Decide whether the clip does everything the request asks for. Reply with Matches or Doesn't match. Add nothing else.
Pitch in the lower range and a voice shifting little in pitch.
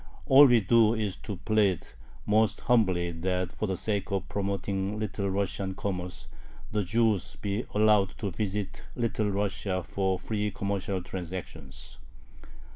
Matches